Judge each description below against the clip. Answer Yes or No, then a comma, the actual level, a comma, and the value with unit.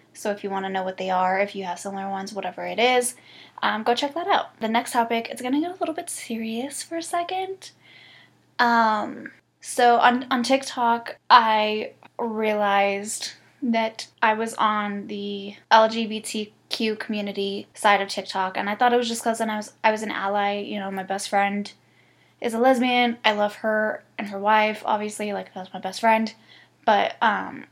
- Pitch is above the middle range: Yes, high, 215 Hz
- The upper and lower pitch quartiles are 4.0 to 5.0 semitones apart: No, average, 3.0 semitones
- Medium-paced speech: Yes, average, 190 wpm